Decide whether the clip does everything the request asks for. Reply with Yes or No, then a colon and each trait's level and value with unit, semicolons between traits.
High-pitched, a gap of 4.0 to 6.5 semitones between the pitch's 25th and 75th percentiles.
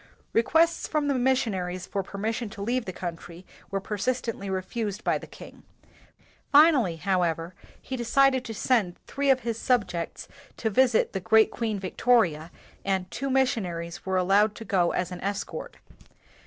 Yes: high, 210 Hz; average, 5.2 semitones